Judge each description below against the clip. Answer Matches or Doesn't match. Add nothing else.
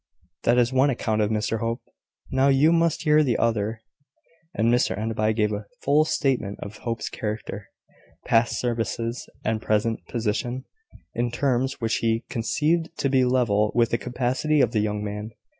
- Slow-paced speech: Doesn't match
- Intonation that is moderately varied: Matches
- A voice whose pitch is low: Matches